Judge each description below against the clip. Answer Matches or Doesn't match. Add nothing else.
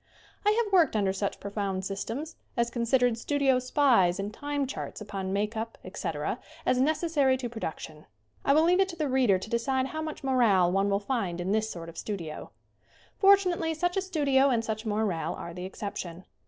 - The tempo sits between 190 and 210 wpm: Matches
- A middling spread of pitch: Doesn't match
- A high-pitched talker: Matches